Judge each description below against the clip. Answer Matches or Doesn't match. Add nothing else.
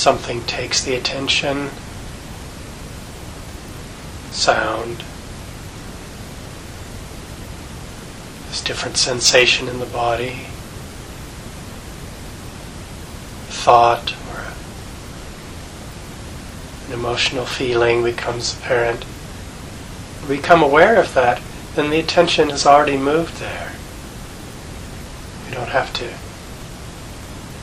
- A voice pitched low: Matches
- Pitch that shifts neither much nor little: Matches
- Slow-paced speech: Matches